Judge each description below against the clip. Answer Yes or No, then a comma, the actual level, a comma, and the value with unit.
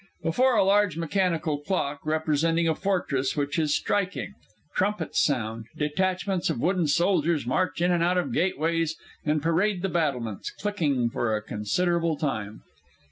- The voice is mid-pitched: Yes, medium, 165 Hz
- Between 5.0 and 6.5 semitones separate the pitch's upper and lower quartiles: No, average, 4.1 semitones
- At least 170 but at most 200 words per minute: No, average, 150 wpm